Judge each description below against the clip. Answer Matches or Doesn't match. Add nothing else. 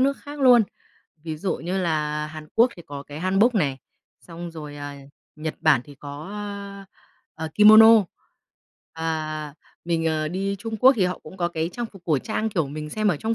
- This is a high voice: Doesn't match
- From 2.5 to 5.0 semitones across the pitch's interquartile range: Doesn't match